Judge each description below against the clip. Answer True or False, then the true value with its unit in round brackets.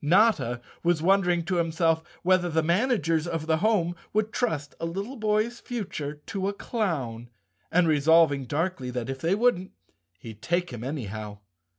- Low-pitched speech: False (165 Hz)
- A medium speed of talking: True (160 wpm)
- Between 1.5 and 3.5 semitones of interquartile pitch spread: False (5.2 semitones)